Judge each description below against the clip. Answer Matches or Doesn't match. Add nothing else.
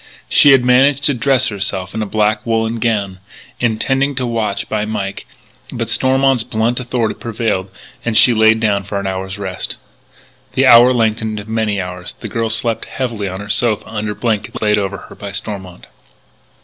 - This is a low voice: Matches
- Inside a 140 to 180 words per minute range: Matches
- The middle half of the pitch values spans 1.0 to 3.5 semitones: Matches